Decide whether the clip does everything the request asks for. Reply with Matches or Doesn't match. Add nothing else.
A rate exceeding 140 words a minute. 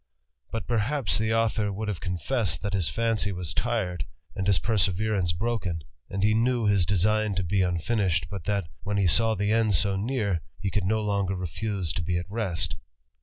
Matches